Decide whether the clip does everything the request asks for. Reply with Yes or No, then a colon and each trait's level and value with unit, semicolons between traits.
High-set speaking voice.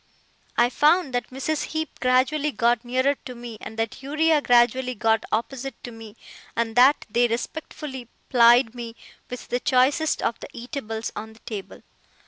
Yes: high, 245 Hz